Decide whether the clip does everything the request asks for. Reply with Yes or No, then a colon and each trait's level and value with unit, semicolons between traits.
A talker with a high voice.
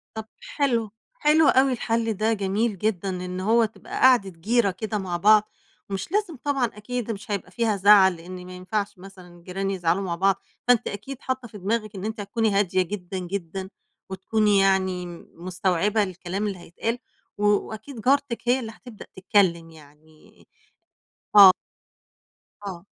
Yes: high, 200 Hz